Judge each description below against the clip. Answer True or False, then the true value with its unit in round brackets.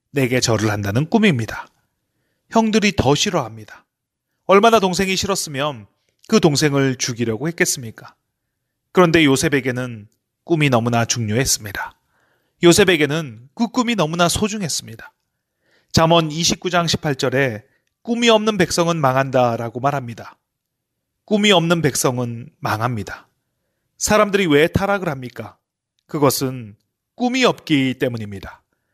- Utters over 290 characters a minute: False (280 characters per minute)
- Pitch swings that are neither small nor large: False (6.7 semitones)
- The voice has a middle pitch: True (145 Hz)